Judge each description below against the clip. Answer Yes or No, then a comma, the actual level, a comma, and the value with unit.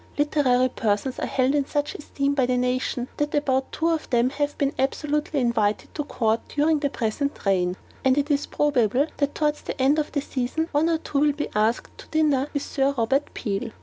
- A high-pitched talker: Yes, very high, 275 Hz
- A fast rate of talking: Yes, fast, 210 wpm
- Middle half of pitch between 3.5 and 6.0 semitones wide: No, average, 2.9 semitones